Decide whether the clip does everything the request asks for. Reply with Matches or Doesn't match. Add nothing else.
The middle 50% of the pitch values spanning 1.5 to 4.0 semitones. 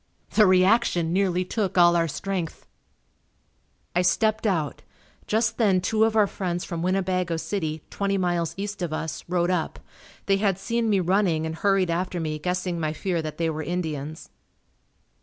Matches